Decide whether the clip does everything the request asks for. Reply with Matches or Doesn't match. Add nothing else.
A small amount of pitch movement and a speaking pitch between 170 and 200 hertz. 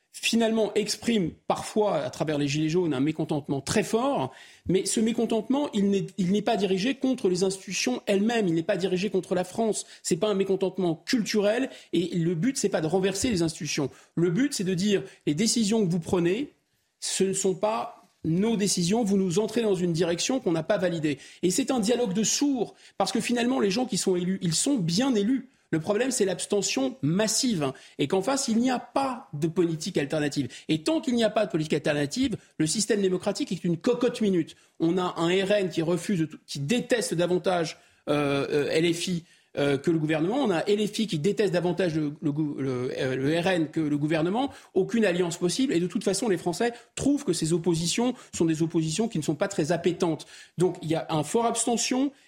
Doesn't match